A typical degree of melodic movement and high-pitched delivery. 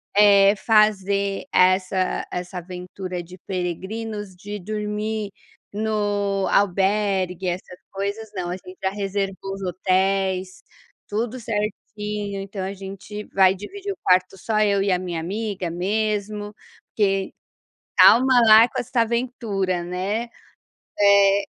No: narrow, 2.2 semitones; high, 200 Hz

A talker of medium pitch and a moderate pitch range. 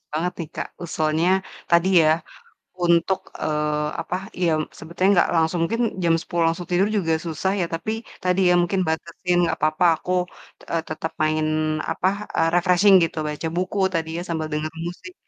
No: medium, 170 Hz; narrow, 2.3 semitones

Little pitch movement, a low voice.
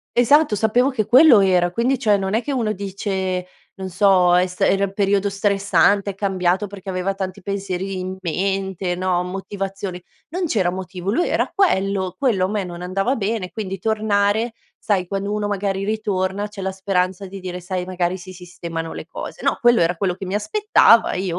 No: narrow, 2.1 semitones; high, 195 Hz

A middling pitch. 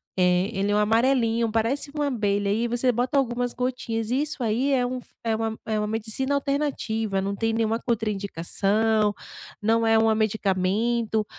No: high, 225 Hz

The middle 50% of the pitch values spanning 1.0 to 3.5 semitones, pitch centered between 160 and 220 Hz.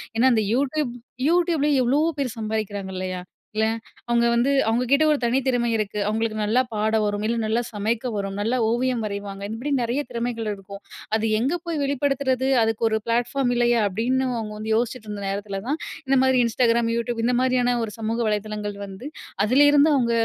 No: average, 3.2 semitones; high, 235 Hz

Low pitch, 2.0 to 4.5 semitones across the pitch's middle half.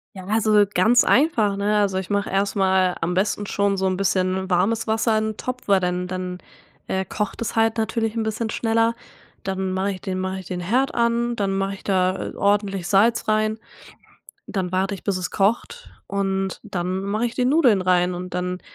No: high, 195 Hz; average, 2.9 semitones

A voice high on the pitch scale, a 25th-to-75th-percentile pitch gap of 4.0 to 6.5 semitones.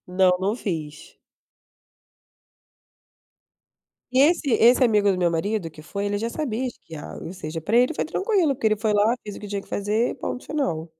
Yes: high, 210 Hz; average, 5.2 semitones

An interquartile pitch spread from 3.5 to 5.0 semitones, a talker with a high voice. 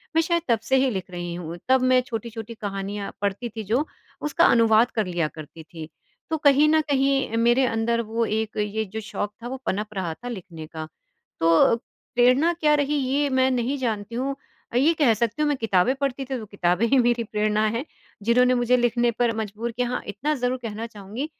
Yes: average, 3.9 semitones; high, 235 Hz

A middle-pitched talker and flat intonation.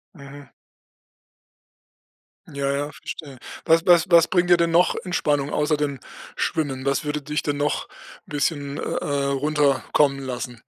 Yes: medium, 145 Hz; narrow, 2.3 semitones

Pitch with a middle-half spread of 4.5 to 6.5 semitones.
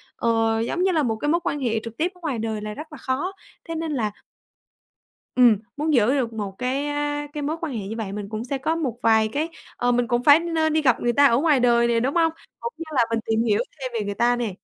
Yes: average, 5.1 semitones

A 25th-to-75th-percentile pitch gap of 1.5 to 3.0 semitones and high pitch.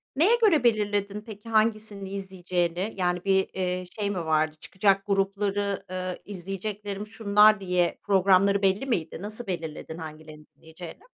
Yes: narrow, 2.5 semitones; high, 195 Hz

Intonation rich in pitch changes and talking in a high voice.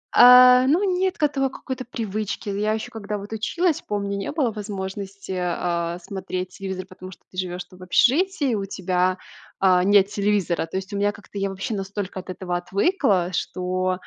No: average, 3.4 semitones; high, 200 Hz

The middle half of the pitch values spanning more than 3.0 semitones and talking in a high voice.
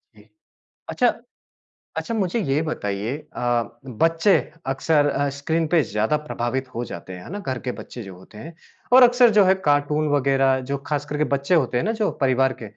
No: average, 5.0 semitones; medium, 140 Hz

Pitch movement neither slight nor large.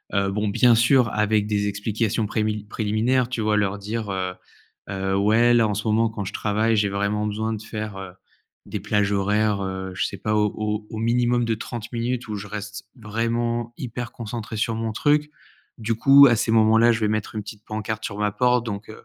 No: narrow, 2.0 semitones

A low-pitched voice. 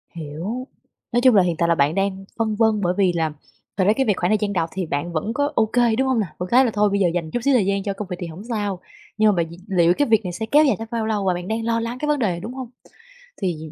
No: high, 200 Hz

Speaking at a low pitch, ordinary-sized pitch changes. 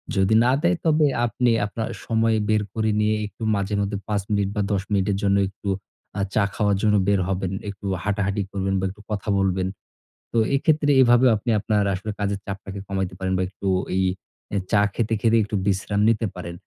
No: low, 100 Hz; narrow, 2.2 semitones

